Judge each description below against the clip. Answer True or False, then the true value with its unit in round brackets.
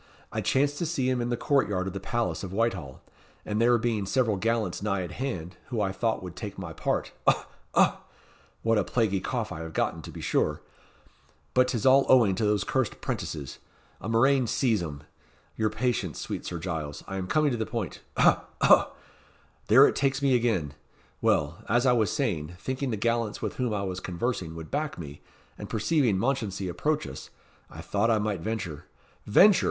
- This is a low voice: True (110 Hz)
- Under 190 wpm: False (200 wpm)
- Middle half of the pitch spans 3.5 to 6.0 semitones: True (5.2 semitones)